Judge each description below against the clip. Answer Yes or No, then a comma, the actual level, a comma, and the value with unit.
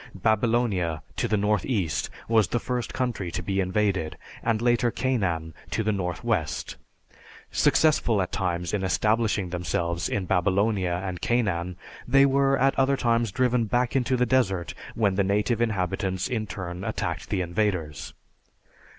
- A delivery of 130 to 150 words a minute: Yes, average, 145 wpm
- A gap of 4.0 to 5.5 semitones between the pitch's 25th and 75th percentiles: Yes, average, 4.6 semitones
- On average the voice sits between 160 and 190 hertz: No, low, 105 Hz